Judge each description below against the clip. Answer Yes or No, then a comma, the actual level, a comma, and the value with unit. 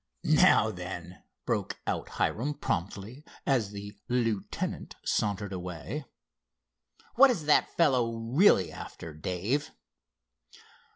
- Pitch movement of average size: No, wide, 6.8 semitones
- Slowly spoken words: Yes, slow, 100 wpm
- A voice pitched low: Yes, low, 110 Hz